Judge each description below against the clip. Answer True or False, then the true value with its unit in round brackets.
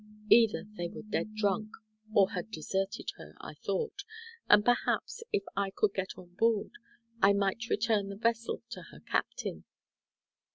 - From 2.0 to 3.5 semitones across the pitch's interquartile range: True (2.4 semitones)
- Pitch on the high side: True (205 Hz)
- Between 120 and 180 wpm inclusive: True (155 wpm)